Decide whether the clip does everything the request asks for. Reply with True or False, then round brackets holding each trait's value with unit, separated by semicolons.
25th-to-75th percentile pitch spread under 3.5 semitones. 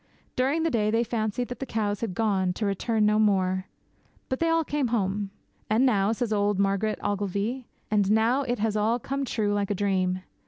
True (3.1 semitones)